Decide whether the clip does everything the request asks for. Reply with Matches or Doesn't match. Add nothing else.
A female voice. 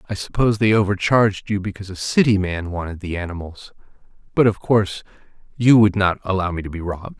Doesn't match